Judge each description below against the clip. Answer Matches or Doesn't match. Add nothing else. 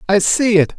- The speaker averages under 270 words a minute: Matches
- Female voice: Doesn't match